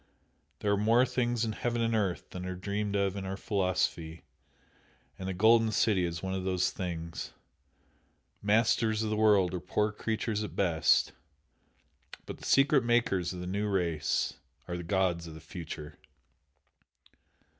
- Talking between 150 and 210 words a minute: Yes, average, 160 wpm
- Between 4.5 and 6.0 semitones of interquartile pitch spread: No, average, 3.5 semitones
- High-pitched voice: No, low, 100 Hz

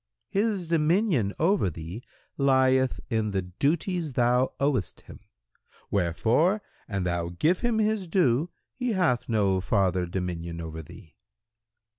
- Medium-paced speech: No, slow, 125 wpm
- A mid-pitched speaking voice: No, low, 125 Hz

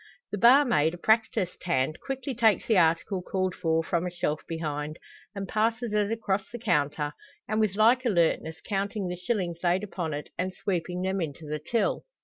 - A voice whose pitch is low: No, medium, 185 Hz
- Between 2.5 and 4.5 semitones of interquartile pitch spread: No, average, 4.9 semitones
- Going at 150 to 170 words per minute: No, average, 180 wpm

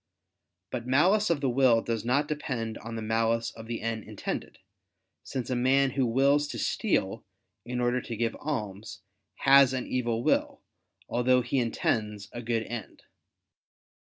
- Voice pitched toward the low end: Yes, low, 120 Hz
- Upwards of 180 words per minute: No, average, 155 wpm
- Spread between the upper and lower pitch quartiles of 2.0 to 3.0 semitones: Yes, average, 2.7 semitones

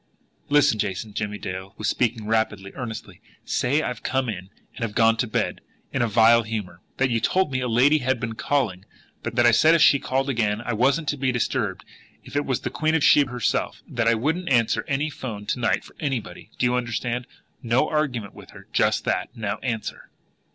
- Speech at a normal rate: No, fast, 215 wpm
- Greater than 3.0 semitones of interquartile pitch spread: Yes, average, 3.4 semitones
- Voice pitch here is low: Yes, low, 120 Hz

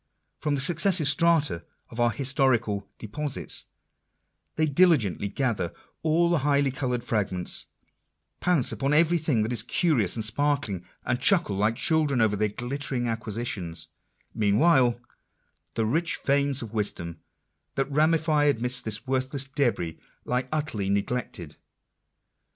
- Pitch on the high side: No, low, 130 Hz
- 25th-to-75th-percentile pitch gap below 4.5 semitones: No, average, 5.3 semitones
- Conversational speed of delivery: No, slow, 130 wpm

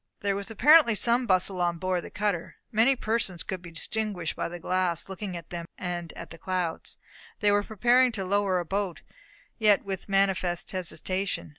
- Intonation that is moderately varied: Yes, average, 3.0 semitones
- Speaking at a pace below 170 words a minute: No, average, 180 wpm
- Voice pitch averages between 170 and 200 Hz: Yes, high, 190 Hz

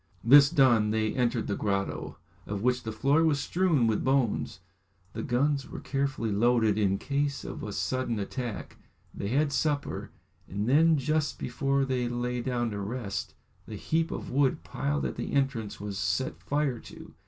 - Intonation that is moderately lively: Yes, average, 4.4 semitones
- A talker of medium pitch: No, low, 125 Hz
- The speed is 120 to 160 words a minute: No, average, 170 wpm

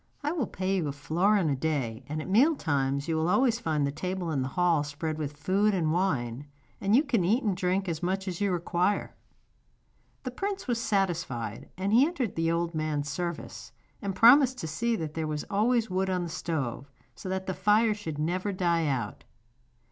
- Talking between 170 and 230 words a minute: Yes, fast, 205 wpm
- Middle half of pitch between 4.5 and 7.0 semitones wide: Yes, average, 4.9 semitones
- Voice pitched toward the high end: No, medium, 180 Hz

